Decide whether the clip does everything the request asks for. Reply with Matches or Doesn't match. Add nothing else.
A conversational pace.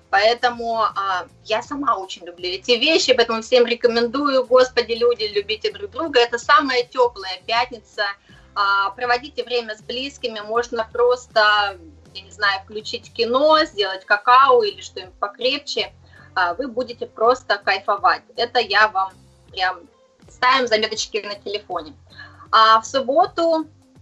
Matches